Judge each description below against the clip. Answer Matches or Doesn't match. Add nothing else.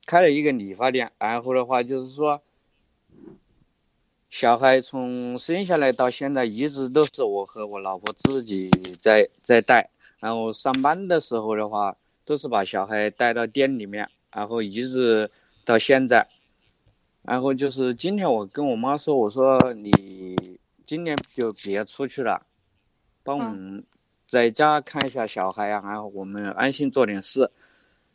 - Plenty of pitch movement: Doesn't match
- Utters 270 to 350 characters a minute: Doesn't match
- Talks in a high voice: Doesn't match